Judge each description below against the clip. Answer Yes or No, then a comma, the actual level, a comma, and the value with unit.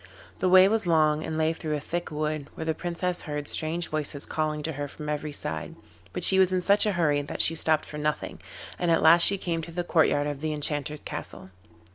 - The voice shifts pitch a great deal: No, narrow, 2.5 semitones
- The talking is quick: Yes, fast, 230 wpm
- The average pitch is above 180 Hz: No, medium, 155 Hz